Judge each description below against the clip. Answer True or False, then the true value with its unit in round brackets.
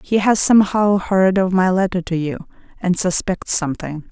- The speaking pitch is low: False (185 Hz)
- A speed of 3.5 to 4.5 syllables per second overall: False (4.9 syllables/s)